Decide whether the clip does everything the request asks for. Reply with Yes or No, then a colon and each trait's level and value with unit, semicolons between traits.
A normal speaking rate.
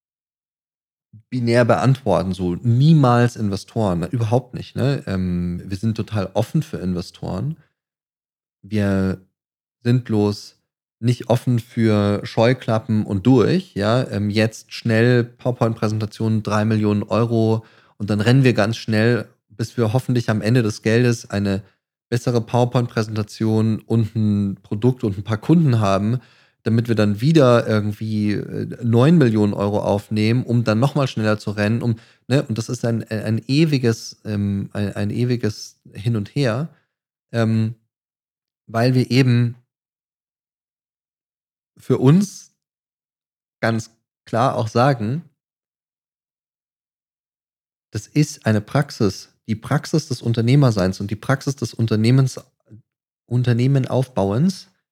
No: slow, 120 wpm